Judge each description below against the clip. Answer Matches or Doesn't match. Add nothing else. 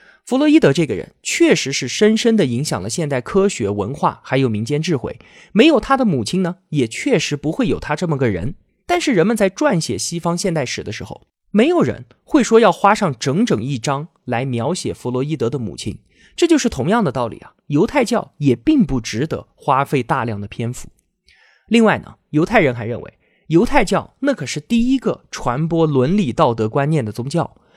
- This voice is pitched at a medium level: Matches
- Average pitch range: Doesn't match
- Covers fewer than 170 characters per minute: Doesn't match